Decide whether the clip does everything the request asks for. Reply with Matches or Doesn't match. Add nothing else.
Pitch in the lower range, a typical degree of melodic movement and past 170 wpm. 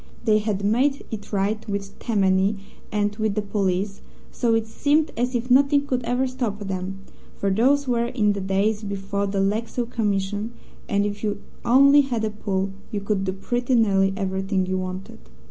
Doesn't match